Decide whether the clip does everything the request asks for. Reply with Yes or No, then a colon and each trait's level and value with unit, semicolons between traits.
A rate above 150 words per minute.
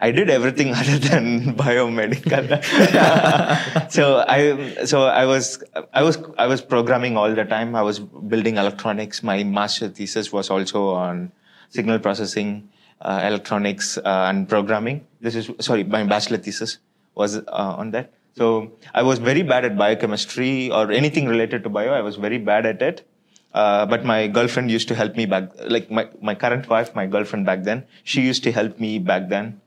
Yes: average, 180 wpm